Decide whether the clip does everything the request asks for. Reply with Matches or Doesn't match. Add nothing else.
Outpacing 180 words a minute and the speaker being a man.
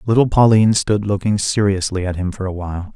Matches